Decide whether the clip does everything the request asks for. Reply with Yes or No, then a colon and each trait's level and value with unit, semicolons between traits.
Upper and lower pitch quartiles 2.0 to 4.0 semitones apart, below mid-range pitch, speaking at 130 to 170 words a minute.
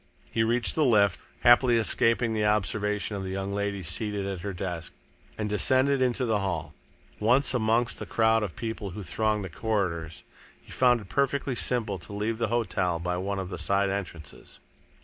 No: average, 3.2 semitones; low, 105 Hz; average, 185 wpm